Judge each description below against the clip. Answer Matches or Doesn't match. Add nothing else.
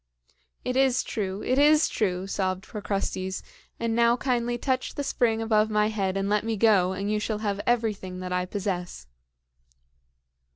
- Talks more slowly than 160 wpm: Doesn't match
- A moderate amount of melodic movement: Matches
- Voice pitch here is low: Doesn't match